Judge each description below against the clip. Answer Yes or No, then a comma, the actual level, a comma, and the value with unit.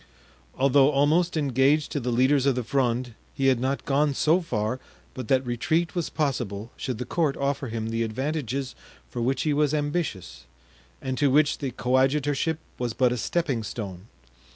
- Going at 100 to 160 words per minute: No, average, 175 wpm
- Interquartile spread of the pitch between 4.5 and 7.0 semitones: No, average, 3.3 semitones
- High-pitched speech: No, low, 135 Hz